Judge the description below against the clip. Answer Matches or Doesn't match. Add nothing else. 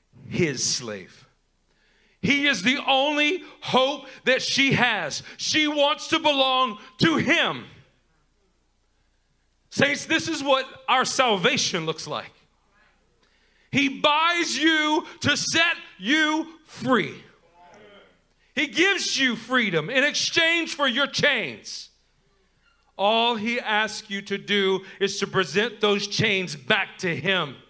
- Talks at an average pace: Doesn't match